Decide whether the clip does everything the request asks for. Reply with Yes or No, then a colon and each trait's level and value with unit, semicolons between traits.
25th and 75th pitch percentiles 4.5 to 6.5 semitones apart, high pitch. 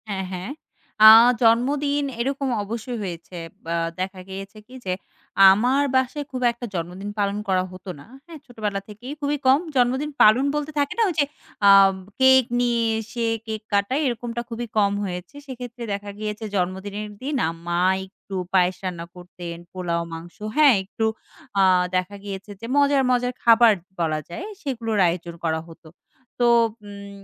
Yes: average, 5.1 semitones; high, 215 Hz